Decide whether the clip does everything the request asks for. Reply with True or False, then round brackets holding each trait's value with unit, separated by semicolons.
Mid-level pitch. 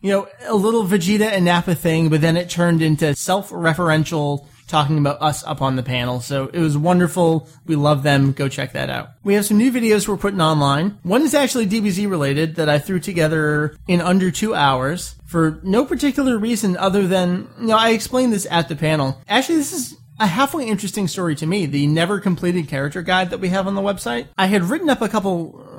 True (175 Hz)